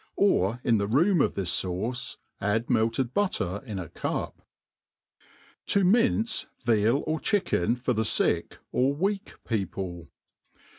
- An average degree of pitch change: No, wide, 8.8 semitones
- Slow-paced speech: Yes, slow, 120 wpm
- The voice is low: Yes, low, 115 Hz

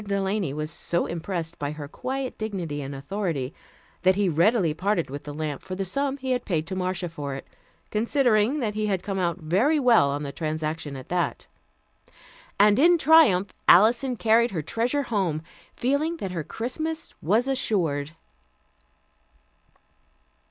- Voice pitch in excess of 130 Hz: Yes, high, 190 Hz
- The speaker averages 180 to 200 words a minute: No, average, 160 wpm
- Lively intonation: Yes, wide, 7.0 semitones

